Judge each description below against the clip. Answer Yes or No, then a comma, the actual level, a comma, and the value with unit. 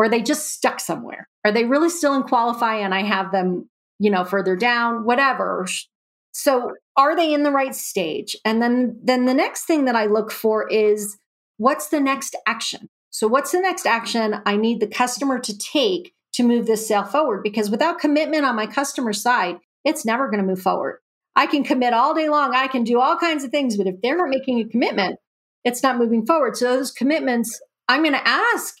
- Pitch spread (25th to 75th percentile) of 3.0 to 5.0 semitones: Yes, average, 4.6 semitones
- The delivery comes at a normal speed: No, fast, 215 wpm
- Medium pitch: No, very high, 250 Hz